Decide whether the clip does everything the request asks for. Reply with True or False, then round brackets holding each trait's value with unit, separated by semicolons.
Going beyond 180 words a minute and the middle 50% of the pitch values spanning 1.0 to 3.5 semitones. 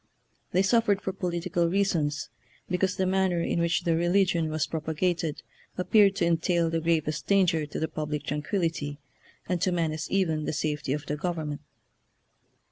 False (170 wpm; 3.0 semitones)